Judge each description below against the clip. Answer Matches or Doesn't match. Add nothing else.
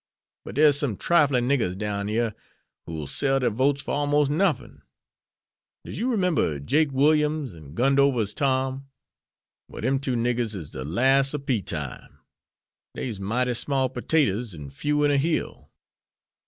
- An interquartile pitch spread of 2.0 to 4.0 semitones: Doesn't match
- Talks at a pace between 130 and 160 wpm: Matches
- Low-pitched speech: Matches